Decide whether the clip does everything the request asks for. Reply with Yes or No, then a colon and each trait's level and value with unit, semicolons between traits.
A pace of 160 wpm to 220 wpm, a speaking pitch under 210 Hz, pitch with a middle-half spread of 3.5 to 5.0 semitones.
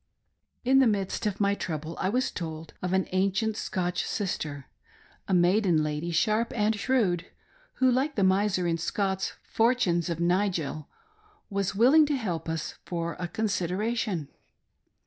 Yes: average, 165 wpm; high, 190 Hz; average, 4.4 semitones